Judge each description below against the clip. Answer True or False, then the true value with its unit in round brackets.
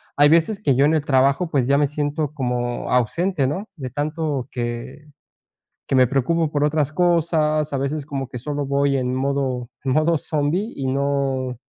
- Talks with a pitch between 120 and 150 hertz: True (140 Hz)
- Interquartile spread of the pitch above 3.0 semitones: False (2.7 semitones)